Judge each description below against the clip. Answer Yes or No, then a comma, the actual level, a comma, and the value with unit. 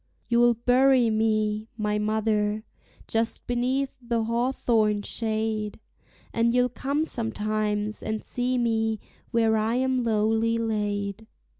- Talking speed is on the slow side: Yes, slow, 115 wpm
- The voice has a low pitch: No, high, 225 Hz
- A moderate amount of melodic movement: No, narrow, 2.0 semitones